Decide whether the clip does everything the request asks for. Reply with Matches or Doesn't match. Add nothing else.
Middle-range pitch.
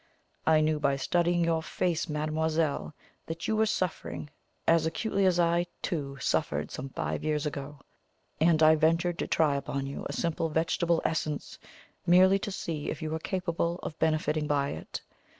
Matches